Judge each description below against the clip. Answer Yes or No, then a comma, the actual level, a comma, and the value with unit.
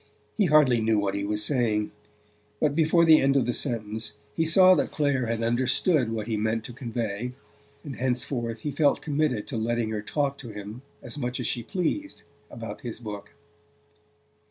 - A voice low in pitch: Yes, low, 120 Hz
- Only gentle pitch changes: No, average, 4.6 semitones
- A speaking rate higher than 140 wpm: Yes, average, 180 wpm